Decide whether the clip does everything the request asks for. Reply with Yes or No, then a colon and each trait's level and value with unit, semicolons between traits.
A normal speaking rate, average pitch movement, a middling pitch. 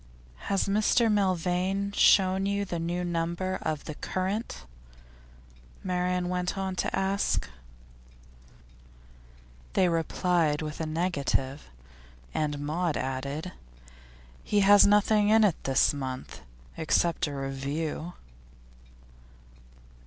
No: slow, 100 wpm; average, 4.0 semitones; medium, 180 Hz